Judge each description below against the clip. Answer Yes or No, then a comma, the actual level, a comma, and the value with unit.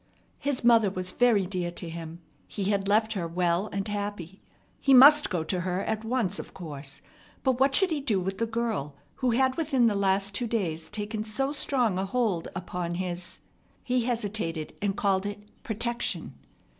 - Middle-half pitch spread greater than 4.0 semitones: Yes, average, 4.6 semitones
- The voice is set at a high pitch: Yes, high, 205 Hz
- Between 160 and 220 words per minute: Yes, average, 180 wpm